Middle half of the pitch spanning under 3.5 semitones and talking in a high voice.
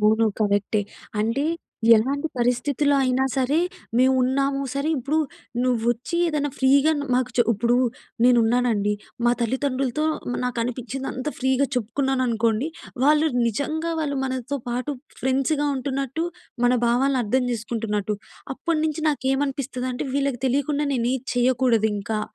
Yes: average, 2.8 semitones; very high, 260 Hz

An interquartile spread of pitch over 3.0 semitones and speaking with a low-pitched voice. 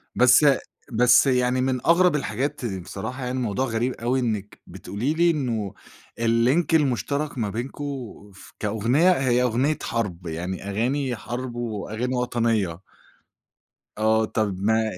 Yes: average, 3.4 semitones; low, 120 Hz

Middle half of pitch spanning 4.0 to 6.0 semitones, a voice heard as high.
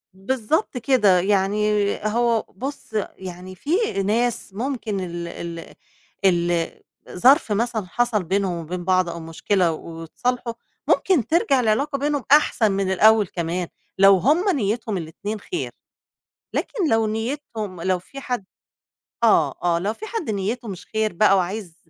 Yes: average, 5.0 semitones; high, 210 Hz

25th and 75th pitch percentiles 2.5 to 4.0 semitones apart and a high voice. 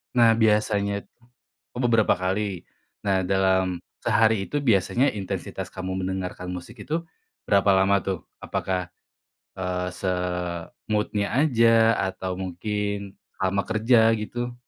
No: average, 3.2 semitones; low, 100 Hz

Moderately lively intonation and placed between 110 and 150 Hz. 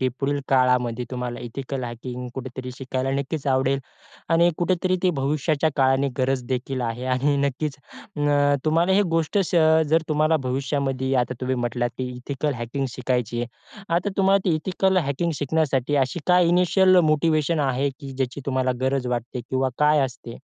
Yes: average, 3.5 semitones; low, 135 Hz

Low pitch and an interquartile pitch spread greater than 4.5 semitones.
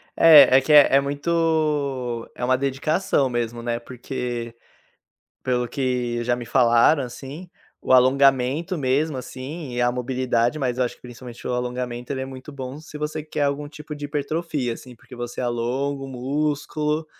No: low, 130 Hz; average, 3.1 semitones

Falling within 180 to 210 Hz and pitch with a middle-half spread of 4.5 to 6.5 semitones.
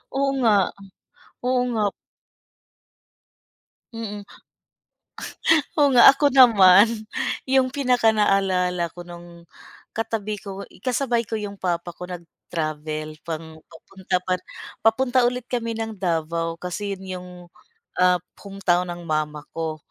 Yes: high, 190 Hz; average, 4.9 semitones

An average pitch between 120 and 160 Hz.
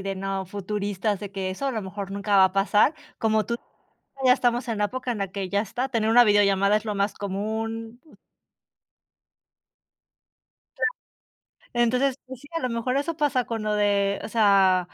No: high, 210 Hz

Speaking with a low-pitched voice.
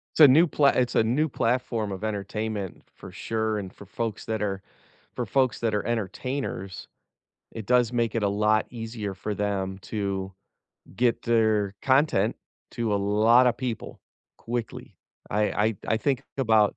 Yes: low, 110 Hz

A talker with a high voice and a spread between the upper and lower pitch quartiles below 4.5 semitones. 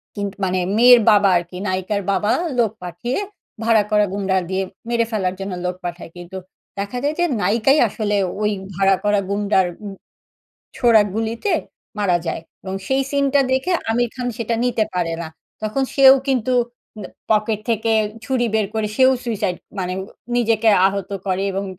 Yes: high, 210 Hz; average, 3.7 semitones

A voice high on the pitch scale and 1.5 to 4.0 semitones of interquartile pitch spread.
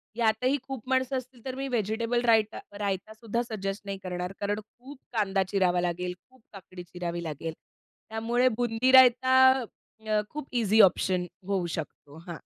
No: high, 215 Hz; average, 4.6 semitones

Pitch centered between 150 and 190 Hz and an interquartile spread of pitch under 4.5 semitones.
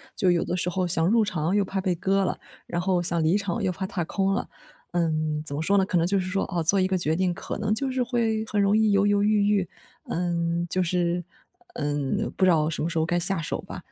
Yes: medium, 185 Hz; average, 3.0 semitones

